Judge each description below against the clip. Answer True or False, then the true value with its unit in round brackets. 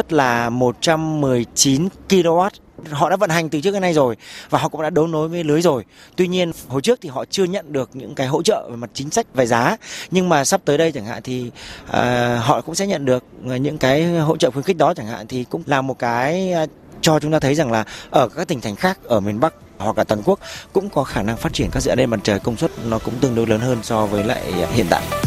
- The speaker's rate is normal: False (260 wpm)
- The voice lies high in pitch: False (145 Hz)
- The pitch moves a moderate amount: False (5.8 semitones)